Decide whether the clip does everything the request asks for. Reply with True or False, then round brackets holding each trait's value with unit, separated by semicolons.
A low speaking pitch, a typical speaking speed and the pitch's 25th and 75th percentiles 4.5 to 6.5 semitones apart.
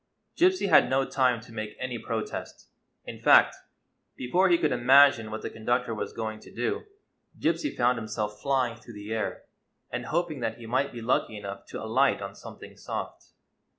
False (120 Hz; 180 wpm; 3.9 semitones)